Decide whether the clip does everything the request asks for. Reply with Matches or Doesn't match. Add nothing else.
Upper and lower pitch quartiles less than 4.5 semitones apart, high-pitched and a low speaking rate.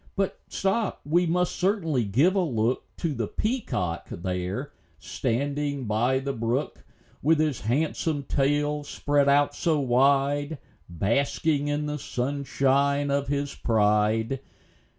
Doesn't match